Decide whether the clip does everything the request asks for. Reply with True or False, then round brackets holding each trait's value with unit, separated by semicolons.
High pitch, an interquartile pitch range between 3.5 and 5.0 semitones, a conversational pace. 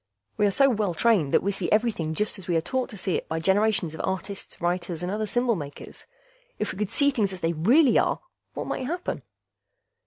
False (195 Hz; 4.6 semitones; 225 wpm)